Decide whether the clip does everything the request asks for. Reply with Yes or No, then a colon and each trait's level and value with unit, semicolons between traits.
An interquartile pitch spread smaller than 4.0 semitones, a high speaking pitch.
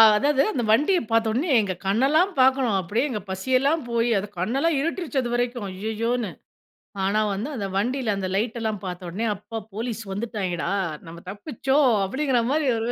No: average, 4.6 semitones; high, 230 Hz